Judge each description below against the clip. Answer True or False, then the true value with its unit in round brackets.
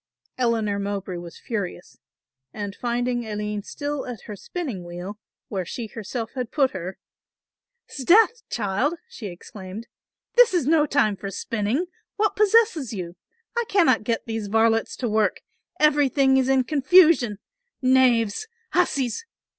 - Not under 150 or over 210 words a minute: False (135 wpm)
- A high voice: True (235 Hz)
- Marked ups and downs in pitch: True (5.8 semitones)